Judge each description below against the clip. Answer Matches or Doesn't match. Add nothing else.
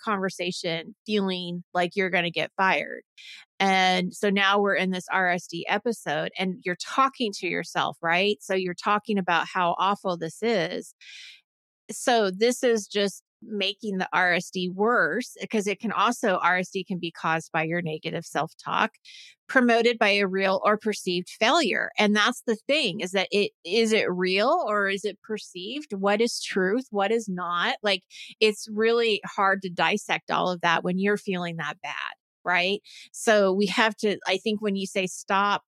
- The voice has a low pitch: Doesn't match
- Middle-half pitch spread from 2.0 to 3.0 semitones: Matches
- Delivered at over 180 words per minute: Doesn't match